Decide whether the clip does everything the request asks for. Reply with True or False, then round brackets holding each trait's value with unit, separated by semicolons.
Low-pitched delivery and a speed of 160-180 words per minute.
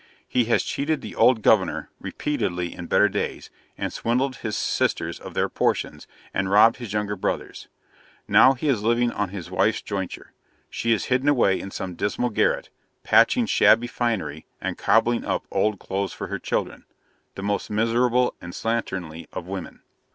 True (110 Hz; 165 wpm)